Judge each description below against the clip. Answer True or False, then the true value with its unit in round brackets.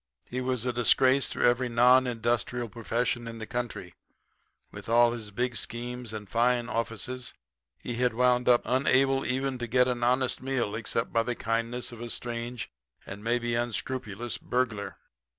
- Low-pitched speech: True (120 Hz)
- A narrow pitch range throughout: True (1.4 semitones)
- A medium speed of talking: True (165 wpm)